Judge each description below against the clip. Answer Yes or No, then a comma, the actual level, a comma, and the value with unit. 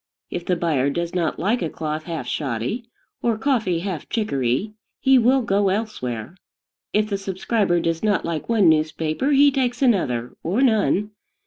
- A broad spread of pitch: Yes, wide, 6.0 semitones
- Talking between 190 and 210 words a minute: No, average, 160 wpm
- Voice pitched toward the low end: No, high, 190 Hz